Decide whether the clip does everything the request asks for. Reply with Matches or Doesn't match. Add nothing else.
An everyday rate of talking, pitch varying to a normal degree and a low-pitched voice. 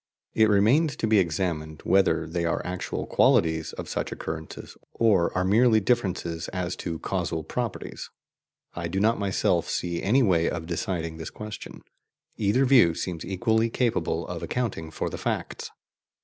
Matches